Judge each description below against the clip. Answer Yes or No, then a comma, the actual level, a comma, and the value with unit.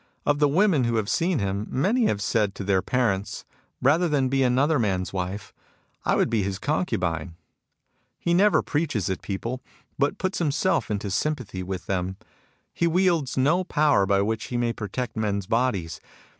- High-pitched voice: No, low, 120 Hz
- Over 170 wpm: Yes, average, 180 wpm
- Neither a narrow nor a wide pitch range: No, wide, 7.2 semitones